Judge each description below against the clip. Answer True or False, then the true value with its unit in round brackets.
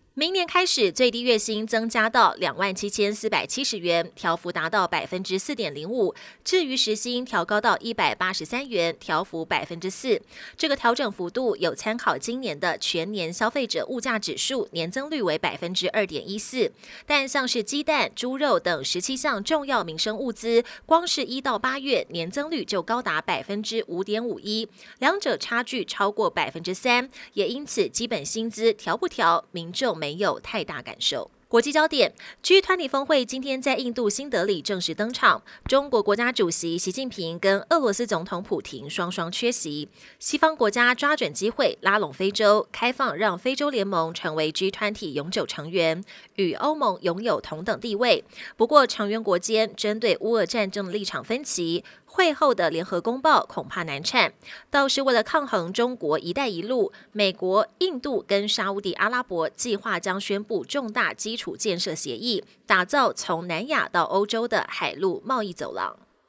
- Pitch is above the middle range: True (220 Hz)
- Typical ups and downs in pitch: False (6.0 semitones)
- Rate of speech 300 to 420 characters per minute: False (275 characters per minute)